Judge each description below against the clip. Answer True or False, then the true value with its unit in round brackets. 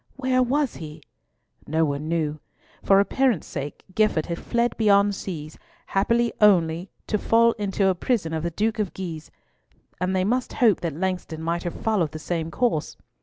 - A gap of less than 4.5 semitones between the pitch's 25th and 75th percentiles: False (5.4 semitones)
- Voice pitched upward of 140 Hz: True (190 Hz)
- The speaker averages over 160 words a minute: True (170 wpm)